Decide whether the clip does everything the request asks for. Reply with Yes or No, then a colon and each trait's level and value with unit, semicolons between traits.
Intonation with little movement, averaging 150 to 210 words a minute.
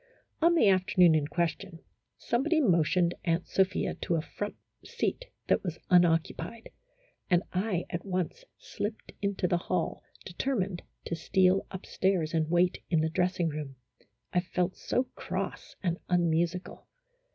No: narrow, 2.3 semitones; average, 140 wpm